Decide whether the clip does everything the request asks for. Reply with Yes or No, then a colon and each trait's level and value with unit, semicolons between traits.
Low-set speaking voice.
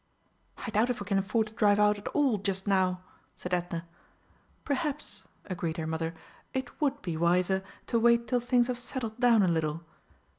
No: high, 205 Hz